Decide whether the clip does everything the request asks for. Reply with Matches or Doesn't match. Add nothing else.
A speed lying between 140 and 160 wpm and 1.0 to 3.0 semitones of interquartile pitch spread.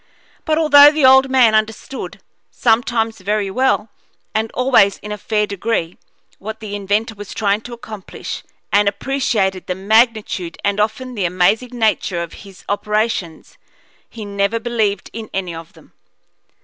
Matches